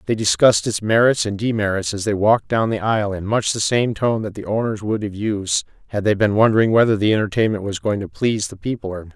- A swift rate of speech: Yes, fast, 250 wpm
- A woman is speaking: No, male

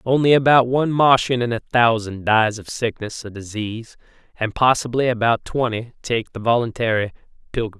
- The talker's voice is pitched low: Yes, low, 120 Hz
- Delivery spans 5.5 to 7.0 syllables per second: Yes, 5.6 syllables/s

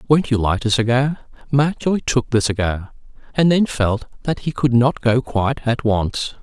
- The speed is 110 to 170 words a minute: No, average, 185 wpm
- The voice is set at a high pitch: No, low, 125 Hz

